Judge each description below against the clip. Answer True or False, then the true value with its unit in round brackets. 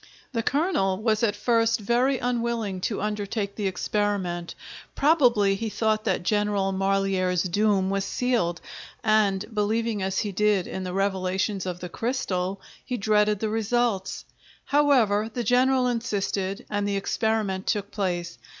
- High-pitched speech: True (205 Hz)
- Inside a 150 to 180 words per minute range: False (140 wpm)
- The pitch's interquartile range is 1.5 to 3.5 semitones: True (2.9 semitones)